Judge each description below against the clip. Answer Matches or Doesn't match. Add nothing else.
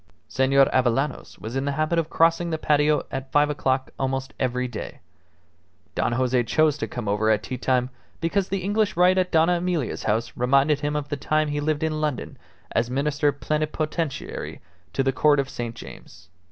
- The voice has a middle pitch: Matches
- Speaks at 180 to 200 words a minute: Matches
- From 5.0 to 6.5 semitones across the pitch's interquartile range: Doesn't match